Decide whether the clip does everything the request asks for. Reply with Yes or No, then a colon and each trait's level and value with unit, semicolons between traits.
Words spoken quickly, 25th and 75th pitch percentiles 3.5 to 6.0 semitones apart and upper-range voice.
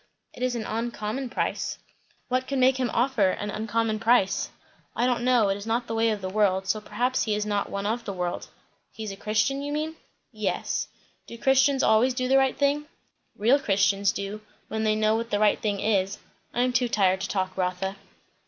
Yes: fast, 210 wpm; average, 3.8 semitones; high, 220 Hz